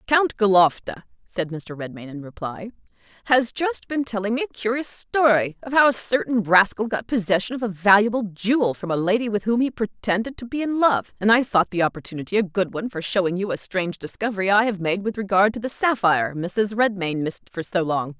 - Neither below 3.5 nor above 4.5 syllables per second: No, 5.8 syllables/s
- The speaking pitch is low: No, high, 205 Hz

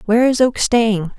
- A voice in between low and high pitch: No, high, 225 Hz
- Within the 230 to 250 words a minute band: No, average, 200 wpm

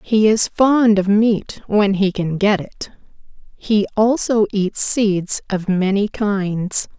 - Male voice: No, female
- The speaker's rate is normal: Yes, average, 145 wpm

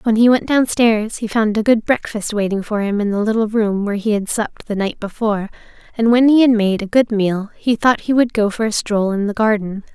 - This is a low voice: No, high, 215 Hz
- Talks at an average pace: No, fast, 255 wpm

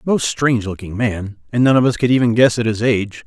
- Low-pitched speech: Yes, low, 115 Hz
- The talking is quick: Yes, fast, 255 wpm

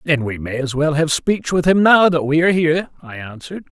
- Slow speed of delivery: No, fast, 255 wpm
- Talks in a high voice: No, medium, 155 Hz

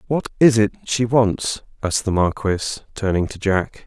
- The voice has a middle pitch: No, low, 105 Hz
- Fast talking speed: No, average, 170 wpm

